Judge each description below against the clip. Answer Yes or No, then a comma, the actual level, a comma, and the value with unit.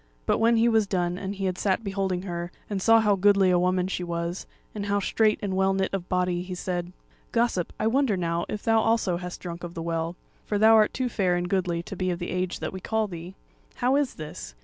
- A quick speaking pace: Yes, fast, 245 wpm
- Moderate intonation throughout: Yes, average, 3.1 semitones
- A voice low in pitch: No, high, 190 Hz